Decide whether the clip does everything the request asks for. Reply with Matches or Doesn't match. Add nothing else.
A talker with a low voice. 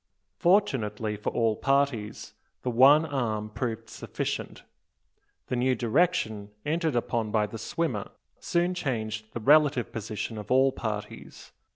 Matches